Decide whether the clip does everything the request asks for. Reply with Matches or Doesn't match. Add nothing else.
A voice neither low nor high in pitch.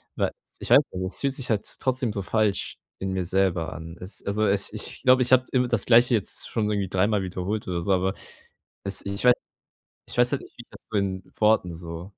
Doesn't match